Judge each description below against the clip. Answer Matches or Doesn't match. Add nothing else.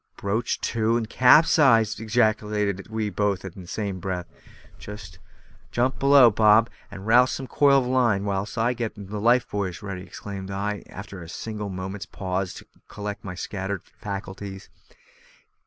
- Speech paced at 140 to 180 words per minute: Matches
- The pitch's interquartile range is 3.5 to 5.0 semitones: Doesn't match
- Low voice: Matches